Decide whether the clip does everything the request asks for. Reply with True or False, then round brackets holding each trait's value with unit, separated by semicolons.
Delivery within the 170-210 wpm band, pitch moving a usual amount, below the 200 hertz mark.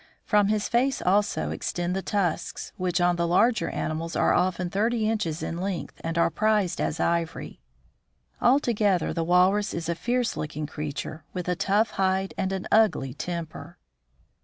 False (160 wpm; 3.6 semitones; 185 Hz)